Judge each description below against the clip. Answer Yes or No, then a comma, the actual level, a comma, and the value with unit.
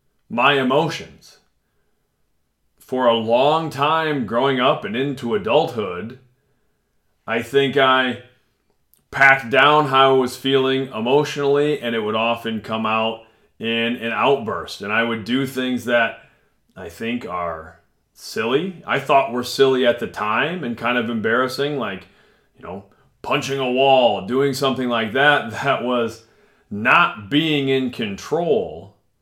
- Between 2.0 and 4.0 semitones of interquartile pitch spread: Yes, average, 2.9 semitones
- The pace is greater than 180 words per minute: No, average, 140 wpm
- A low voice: Yes, low, 125 Hz